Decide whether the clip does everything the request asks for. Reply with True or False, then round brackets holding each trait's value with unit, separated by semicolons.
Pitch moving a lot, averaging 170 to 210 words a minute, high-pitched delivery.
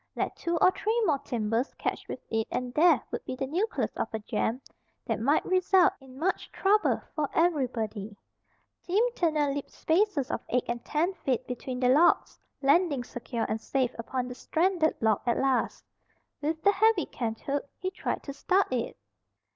True (6.0 semitones; 175 wpm; 280 Hz)